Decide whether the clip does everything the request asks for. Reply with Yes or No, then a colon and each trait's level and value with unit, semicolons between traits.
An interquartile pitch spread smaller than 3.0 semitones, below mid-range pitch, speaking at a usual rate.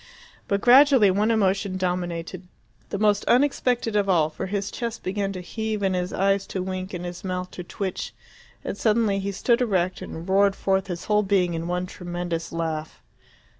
No: narrow, 2.6 semitones; high, 190 Hz; average, 180 wpm